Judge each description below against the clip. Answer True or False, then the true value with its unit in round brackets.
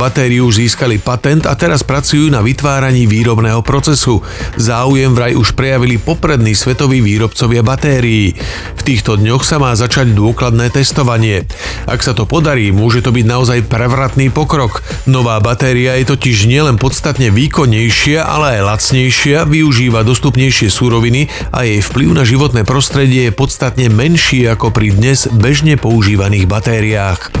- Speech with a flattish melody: False (3.3 semitones)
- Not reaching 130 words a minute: False (140 wpm)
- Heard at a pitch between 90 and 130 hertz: True (125 Hz)